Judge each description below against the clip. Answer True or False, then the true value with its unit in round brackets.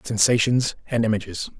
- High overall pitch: False (110 Hz)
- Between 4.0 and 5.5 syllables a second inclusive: True (5.2 syllables/s)